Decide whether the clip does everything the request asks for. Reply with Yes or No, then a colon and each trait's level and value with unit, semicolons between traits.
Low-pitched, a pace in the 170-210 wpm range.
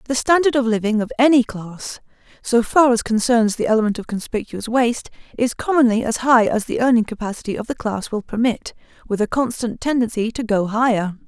No: high, 235 Hz; average, 185 wpm